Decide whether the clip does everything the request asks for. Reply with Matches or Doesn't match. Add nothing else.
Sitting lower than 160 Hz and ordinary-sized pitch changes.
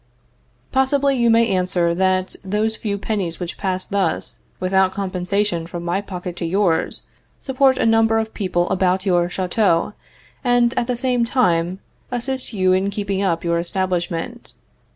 Doesn't match